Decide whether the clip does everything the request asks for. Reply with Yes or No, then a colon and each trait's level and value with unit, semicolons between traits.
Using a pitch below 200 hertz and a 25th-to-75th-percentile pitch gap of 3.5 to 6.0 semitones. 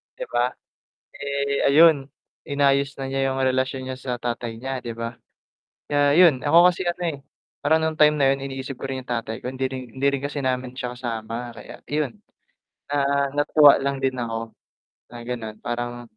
No: low, 135 Hz; average, 2.7 semitones